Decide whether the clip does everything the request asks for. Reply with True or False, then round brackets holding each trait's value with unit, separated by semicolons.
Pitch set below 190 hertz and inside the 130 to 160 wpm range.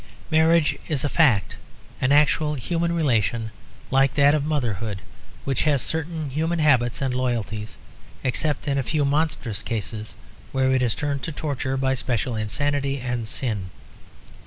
True (135 Hz; 150 wpm)